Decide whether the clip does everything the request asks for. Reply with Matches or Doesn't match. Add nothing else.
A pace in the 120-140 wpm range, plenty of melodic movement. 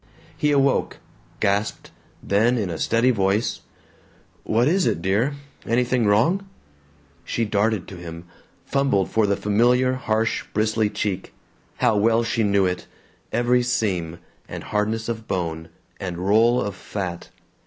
Doesn't match